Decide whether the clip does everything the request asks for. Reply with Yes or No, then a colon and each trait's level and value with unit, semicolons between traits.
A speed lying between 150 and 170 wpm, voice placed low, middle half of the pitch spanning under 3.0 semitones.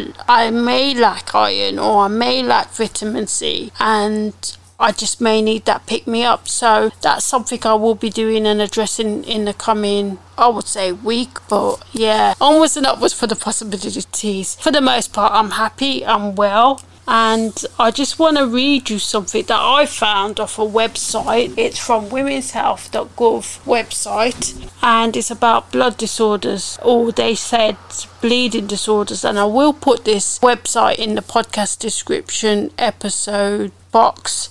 No: average, 160 wpm; high, 225 Hz; narrow, 2.4 semitones